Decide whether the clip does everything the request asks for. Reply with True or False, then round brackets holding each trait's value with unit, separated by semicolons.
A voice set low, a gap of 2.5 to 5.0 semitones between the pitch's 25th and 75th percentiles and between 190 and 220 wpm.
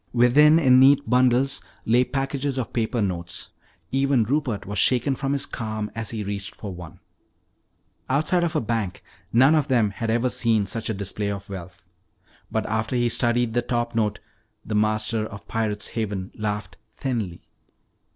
False (115 Hz; 3.6 semitones; 165 wpm)